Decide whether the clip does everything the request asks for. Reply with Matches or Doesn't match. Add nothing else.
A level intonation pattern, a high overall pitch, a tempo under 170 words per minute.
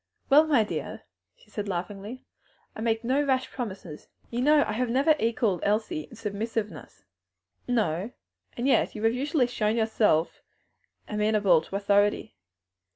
Doesn't match